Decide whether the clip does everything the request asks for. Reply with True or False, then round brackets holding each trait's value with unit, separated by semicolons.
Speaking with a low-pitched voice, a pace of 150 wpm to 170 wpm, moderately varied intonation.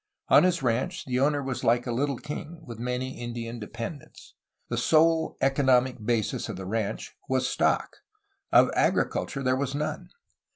True (130 Hz; 160 wpm; 3.4 semitones)